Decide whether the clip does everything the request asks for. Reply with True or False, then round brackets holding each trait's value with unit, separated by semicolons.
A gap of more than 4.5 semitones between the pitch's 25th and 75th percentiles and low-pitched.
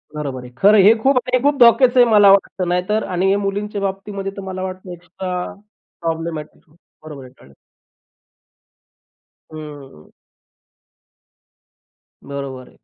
False (4.9 semitones; 185 Hz)